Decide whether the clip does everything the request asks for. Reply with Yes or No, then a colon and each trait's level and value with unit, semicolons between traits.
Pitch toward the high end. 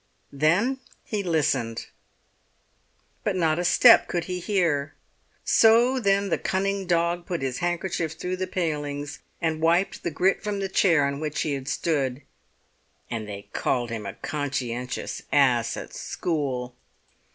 No: medium, 160 Hz